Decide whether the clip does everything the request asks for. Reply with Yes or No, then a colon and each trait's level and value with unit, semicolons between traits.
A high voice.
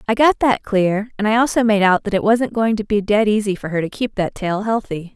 Yes: high, 210 Hz